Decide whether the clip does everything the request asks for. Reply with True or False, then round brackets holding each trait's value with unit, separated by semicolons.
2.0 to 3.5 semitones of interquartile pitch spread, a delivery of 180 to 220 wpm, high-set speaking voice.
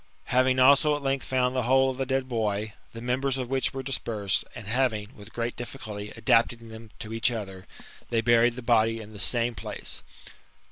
False (2.8 semitones; 195 wpm; 120 Hz)